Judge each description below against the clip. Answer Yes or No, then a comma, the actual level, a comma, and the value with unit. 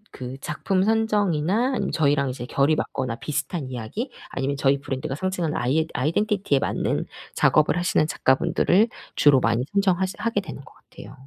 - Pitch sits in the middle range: Yes, medium, 150 Hz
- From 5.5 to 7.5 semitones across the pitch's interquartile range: Yes, wide, 6.0 semitones